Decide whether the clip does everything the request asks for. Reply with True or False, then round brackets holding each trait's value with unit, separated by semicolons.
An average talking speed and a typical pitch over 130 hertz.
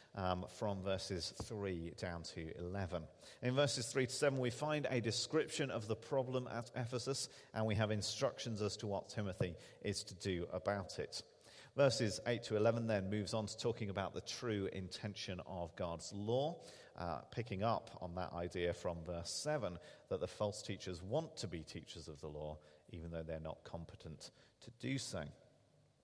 False (180 wpm; 105 Hz)